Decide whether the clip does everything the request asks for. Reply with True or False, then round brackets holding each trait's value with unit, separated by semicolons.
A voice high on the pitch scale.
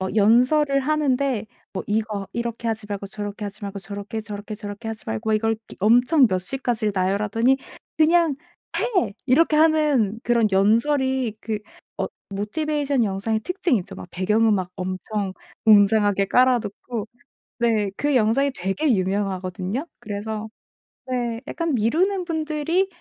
True (225 Hz)